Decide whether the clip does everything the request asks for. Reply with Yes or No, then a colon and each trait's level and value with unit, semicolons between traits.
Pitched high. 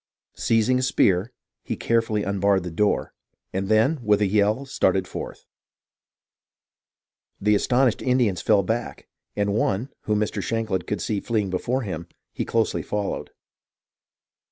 No: low, 105 Hz